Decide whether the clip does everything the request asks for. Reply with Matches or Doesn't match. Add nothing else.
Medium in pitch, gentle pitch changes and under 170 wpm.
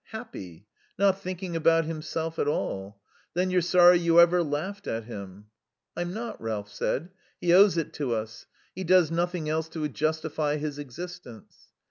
Doesn't match